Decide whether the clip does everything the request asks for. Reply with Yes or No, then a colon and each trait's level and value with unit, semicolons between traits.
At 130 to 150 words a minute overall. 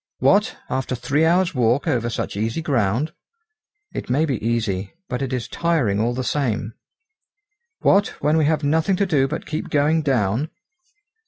No: average, 165 wpm